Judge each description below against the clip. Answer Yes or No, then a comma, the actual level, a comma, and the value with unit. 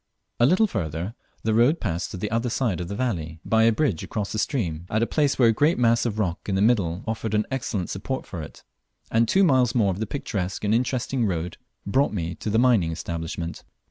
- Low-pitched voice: Yes, low, 110 Hz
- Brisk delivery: Yes, fast, 230 wpm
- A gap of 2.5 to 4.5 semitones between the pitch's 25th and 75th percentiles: No, wide, 5.4 semitones